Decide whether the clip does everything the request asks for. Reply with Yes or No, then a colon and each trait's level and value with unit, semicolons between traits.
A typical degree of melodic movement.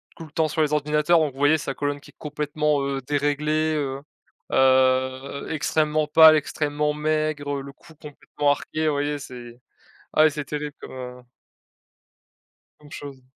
No: narrow, 1.7 semitones